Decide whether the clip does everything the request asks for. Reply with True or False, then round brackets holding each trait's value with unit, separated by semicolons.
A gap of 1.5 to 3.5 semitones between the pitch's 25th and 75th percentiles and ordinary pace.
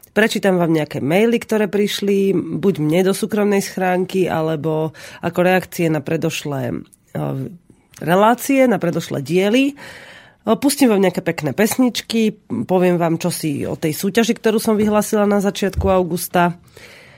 False (4.3 semitones; 130 wpm)